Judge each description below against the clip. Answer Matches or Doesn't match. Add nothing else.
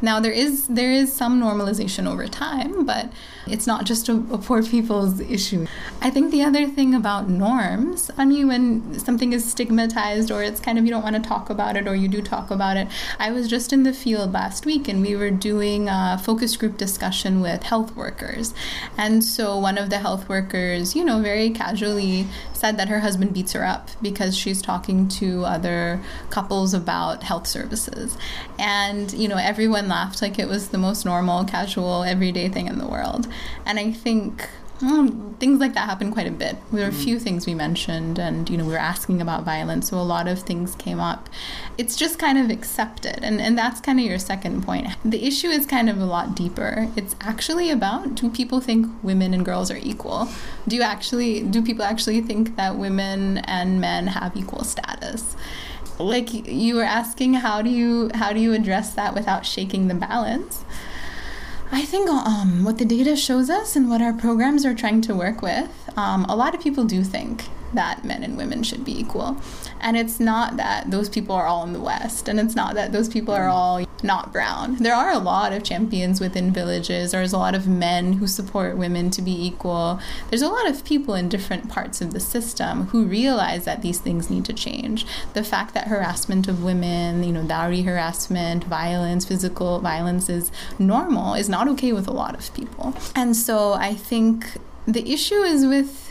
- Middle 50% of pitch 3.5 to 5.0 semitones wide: Matches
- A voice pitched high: Matches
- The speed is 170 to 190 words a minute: Doesn't match